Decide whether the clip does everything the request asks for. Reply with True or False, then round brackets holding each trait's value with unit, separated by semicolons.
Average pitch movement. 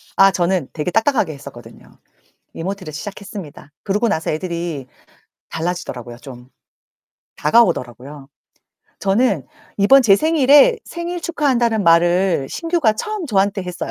False (7.0 semitones)